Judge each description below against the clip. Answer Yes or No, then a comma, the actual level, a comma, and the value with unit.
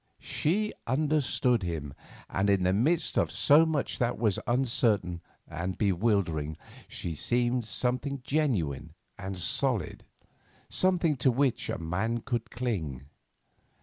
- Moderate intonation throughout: No, wide, 6.9 semitones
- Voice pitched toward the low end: Yes, low, 115 Hz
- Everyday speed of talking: No, slow, 120 wpm